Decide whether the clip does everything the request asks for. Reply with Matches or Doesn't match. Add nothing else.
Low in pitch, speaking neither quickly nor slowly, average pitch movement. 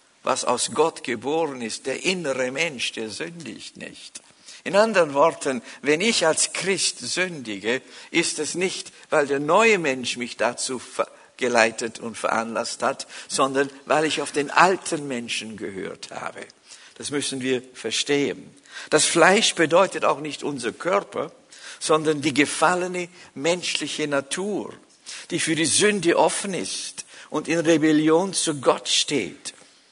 Doesn't match